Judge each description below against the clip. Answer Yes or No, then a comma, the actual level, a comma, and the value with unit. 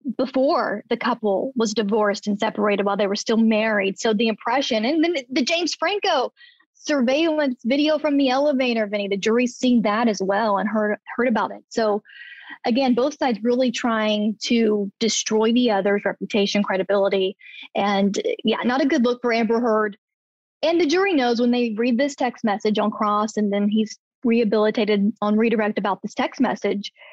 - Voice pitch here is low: No, high, 230 Hz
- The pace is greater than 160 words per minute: Yes, average, 175 wpm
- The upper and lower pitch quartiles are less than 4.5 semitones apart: Yes, average, 3.9 semitones